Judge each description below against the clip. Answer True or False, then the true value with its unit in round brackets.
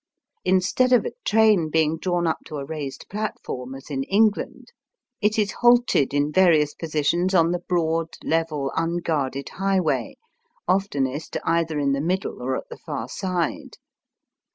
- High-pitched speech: False (165 Hz)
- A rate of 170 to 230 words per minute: False (150 wpm)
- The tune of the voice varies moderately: True (4.3 semitones)